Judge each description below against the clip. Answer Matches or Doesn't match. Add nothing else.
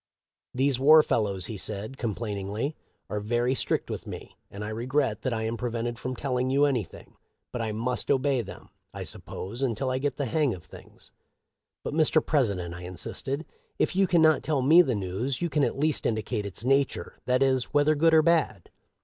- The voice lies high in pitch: Doesn't match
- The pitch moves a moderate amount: Matches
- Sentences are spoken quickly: Matches